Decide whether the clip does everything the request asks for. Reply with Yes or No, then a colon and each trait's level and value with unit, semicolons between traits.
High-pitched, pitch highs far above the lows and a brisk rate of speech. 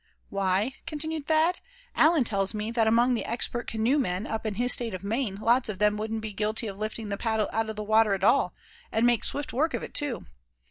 No: high, 225 Hz; average, 2.8 semitones; fast, 225 wpm